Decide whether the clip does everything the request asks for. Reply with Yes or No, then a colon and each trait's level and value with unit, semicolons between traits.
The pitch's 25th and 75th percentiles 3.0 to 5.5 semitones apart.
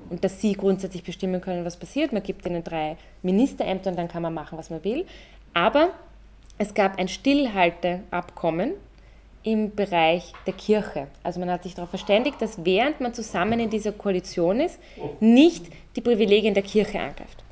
Yes: average, 3.8 semitones